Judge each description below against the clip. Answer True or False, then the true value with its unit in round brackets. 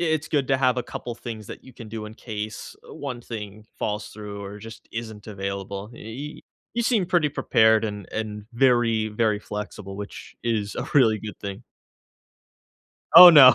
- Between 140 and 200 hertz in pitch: False (110 Hz)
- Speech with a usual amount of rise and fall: True (3.2 semitones)